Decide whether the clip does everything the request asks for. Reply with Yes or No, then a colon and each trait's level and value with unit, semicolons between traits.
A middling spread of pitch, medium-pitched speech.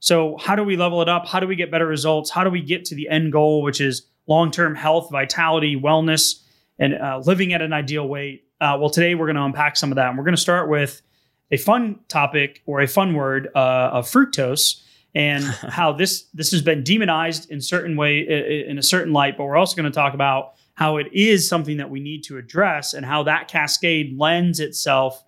Yes: average, 3.2 semitones; medium, 150 Hz